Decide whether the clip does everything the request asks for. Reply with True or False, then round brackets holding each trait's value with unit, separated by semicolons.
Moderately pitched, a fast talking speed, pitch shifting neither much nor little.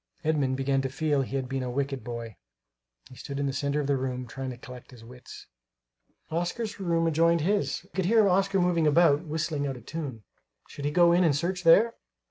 True (145 Hz; 215 wpm; 4.3 semitones)